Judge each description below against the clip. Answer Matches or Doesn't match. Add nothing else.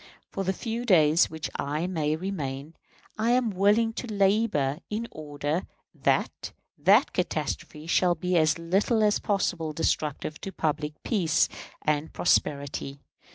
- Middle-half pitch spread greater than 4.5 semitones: Matches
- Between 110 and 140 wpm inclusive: Matches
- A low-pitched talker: Doesn't match